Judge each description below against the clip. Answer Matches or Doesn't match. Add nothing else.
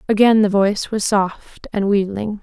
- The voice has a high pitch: Matches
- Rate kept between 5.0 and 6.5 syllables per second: Doesn't match